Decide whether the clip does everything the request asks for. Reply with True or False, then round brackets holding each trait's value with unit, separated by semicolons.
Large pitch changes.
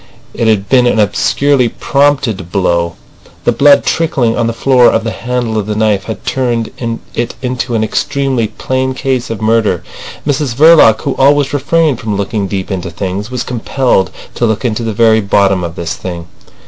False (4.3 semitones)